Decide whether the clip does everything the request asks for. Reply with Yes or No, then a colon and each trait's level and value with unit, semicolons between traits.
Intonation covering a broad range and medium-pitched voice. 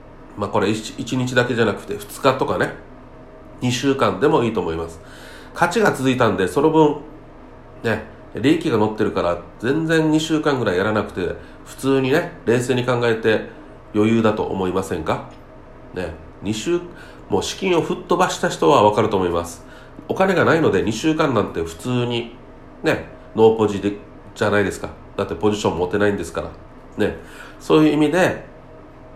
No: wide, 6.7 semitones; low, 120 Hz